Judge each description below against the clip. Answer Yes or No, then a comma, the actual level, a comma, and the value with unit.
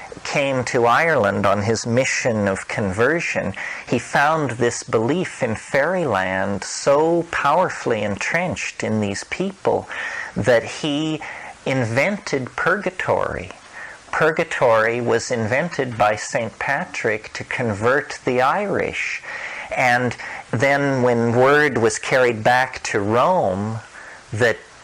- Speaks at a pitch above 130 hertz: No, low, 125 Hz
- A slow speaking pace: Yes, slow, 105 wpm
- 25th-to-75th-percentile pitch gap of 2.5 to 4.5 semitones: Yes, average, 4.1 semitones